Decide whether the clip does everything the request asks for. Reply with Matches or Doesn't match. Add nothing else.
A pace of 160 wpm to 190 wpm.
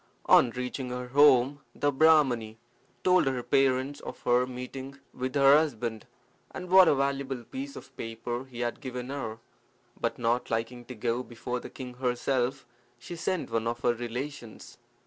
Matches